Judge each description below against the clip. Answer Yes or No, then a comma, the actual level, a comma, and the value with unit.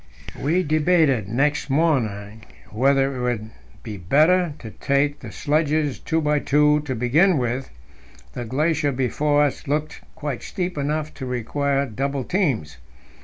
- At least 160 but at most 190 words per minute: No, average, 145 wpm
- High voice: No, medium, 140 Hz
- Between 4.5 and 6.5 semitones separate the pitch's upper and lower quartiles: No, average, 3.5 semitones